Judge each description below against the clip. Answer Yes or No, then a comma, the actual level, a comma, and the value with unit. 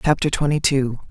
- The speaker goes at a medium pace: Yes, average, 160 wpm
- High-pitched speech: No, medium, 140 Hz